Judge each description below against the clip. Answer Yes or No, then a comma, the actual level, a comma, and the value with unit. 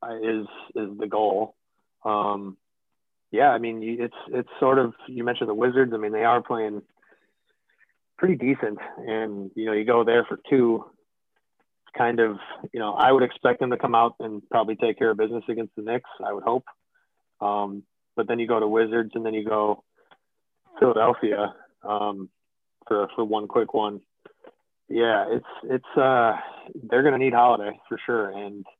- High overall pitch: No, low, 110 Hz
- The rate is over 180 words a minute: No, average, 175 wpm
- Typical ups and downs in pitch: No, narrow, 2.3 semitones